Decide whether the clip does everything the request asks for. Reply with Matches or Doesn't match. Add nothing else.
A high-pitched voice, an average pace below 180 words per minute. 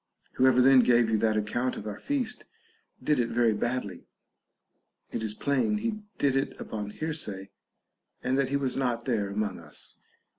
Doesn't match